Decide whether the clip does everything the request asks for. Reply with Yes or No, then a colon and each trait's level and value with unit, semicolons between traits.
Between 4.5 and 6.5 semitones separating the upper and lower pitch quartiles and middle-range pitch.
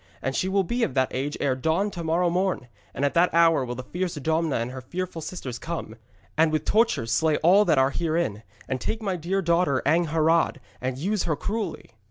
Yes: average, 5.2 semitones; medium, 165 Hz